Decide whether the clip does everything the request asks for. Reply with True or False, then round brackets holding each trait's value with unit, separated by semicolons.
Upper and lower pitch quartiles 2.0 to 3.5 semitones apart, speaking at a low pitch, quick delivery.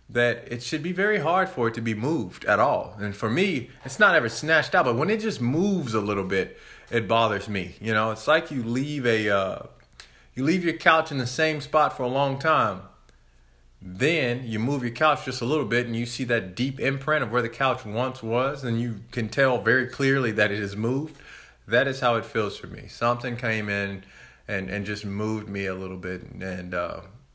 False (4.8 semitones; 120 Hz; 230 wpm)